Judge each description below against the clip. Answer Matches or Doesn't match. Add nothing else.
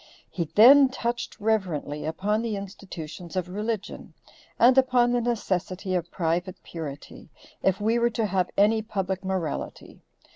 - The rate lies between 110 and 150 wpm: Matches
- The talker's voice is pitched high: Matches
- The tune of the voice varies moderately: Matches